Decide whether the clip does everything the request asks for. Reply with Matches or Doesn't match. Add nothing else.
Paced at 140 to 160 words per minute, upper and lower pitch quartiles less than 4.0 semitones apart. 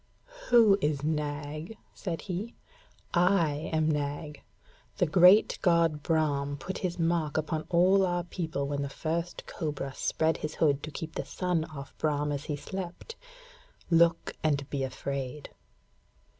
Matches